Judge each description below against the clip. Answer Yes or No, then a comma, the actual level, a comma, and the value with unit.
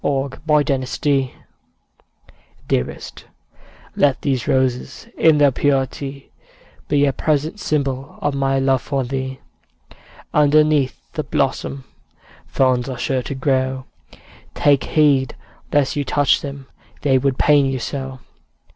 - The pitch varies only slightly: Yes, narrow, 1.6 semitones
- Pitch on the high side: No, low, 135 Hz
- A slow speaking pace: Yes, slow, 125 wpm